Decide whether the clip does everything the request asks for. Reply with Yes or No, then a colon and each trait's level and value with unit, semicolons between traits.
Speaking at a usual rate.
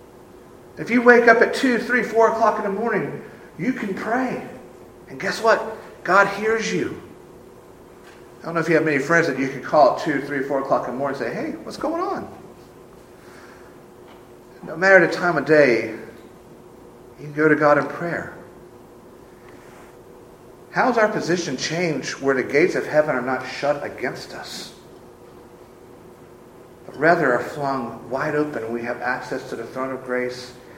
Yes: average, 175 wpm